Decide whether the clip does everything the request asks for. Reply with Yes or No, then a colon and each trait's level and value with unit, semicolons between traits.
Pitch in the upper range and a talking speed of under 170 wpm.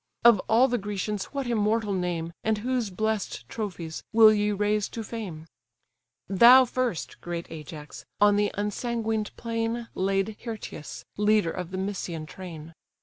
Yes: high, 210 Hz; average, 145 wpm